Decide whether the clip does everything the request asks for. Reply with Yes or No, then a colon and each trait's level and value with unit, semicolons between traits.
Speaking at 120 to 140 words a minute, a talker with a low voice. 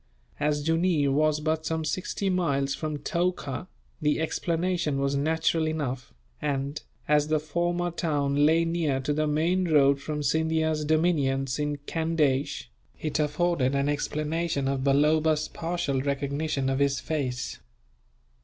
No: slow, 135 wpm; medium, 150 Hz